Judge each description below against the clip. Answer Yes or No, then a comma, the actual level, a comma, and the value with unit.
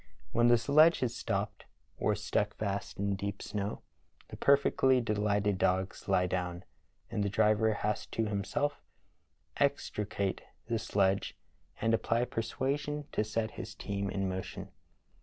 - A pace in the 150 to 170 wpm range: No, average, 140 wpm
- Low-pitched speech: Yes, low, 105 Hz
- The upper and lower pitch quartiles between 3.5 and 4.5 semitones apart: No, average, 2.7 semitones